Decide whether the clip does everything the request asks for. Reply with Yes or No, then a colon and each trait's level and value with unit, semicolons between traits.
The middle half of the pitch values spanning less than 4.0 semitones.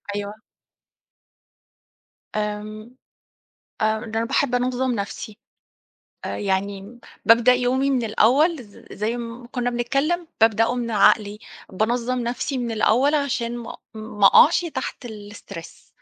Yes: average, 2.9 semitones